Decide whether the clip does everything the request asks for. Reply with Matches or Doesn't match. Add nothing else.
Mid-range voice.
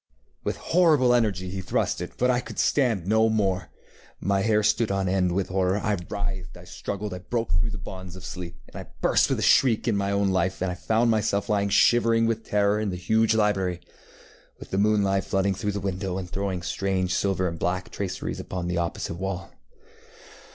Doesn't match